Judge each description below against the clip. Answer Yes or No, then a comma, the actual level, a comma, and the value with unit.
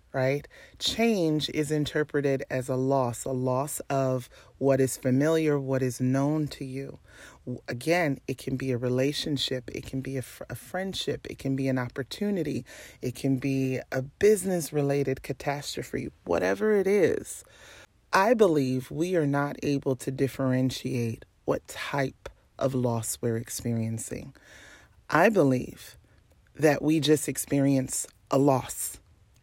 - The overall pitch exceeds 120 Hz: Yes, low, 135 Hz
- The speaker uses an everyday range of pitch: No, narrow, 2.1 semitones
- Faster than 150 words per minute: No, slow, 135 wpm